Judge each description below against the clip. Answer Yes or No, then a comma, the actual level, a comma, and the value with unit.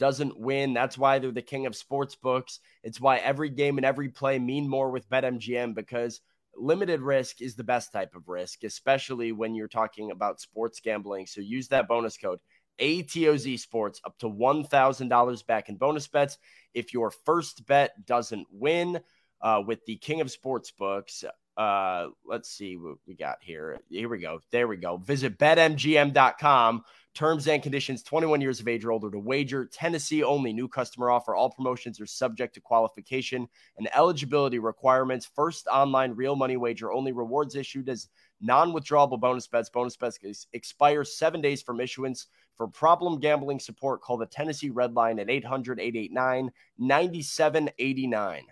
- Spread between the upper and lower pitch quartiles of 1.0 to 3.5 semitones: Yes, average, 3.2 semitones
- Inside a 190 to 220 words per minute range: No, average, 170 wpm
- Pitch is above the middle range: No, low, 130 Hz